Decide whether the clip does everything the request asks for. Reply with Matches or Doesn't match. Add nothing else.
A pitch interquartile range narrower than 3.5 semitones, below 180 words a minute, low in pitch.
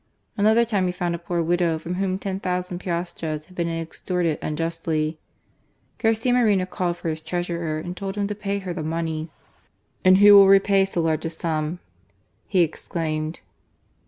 Doesn't match